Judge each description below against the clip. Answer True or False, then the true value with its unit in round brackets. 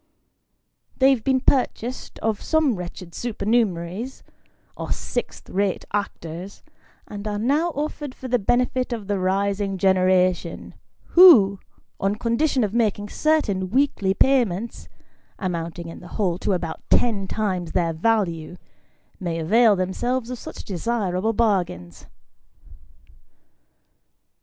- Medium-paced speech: False (120 wpm)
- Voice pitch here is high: True (205 Hz)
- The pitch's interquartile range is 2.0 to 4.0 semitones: False (4.7 semitones)